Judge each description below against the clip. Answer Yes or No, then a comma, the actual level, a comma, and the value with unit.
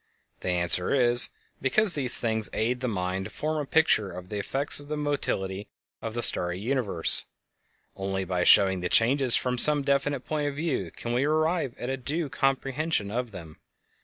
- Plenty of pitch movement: Yes, wide, 6.7 semitones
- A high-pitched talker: No, low, 125 Hz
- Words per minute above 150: Yes, average, 185 wpm